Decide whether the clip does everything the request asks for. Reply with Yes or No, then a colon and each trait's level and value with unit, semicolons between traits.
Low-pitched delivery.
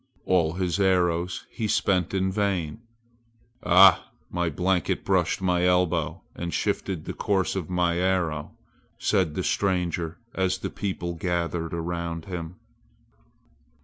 Yes: very low, 90 Hz